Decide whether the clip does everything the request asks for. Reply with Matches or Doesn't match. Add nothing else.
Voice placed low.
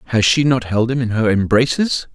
Matches